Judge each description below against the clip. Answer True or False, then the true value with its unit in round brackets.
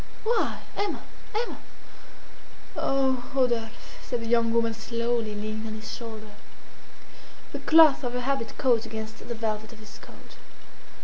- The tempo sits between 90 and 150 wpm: True (140 wpm)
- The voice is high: True (230 Hz)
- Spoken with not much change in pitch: True (2.3 semitones)